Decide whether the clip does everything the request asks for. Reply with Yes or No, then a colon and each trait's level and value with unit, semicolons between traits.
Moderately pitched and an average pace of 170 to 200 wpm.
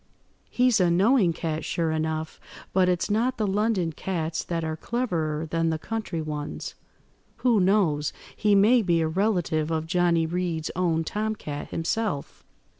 No: medium, 170 Hz; average, 150 wpm